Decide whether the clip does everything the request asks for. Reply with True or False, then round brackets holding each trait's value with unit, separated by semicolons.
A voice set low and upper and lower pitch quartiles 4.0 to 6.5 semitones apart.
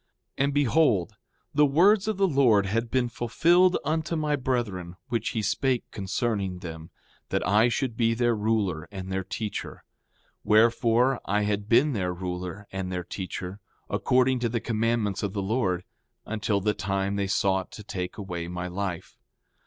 True (105 Hz; 4.6 semitones)